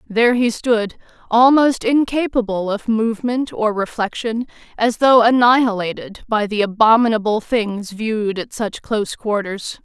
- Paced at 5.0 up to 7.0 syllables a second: No, 4.5 syllables/s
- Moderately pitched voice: No, high, 225 Hz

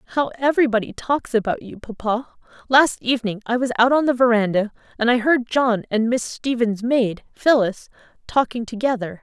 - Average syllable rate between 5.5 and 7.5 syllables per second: No, 5.2 syllables/s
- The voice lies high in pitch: Yes, high, 235 Hz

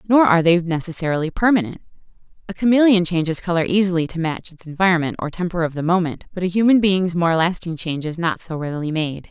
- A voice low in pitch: No, medium, 175 Hz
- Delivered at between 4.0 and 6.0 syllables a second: No, 6.5 syllables/s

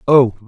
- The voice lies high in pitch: No, low, 120 Hz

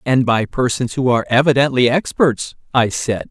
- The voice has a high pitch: No, low, 125 Hz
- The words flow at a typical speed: Yes, average, 165 wpm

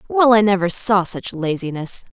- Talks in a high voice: Yes, high, 200 Hz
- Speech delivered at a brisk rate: No, average, 170 wpm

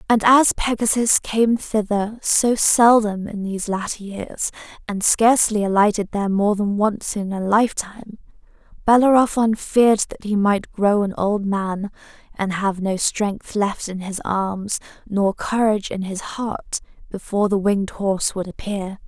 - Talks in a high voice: Yes, high, 210 Hz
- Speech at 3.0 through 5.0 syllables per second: Yes, 4.4 syllables/s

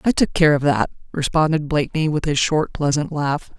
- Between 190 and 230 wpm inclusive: Yes, average, 200 wpm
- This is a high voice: No, medium, 150 Hz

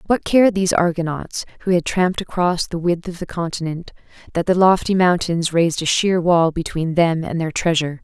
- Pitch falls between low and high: Yes, medium, 170 Hz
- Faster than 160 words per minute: Yes, average, 195 wpm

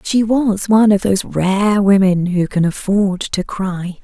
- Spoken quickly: No, average, 180 wpm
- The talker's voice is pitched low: No, high, 195 Hz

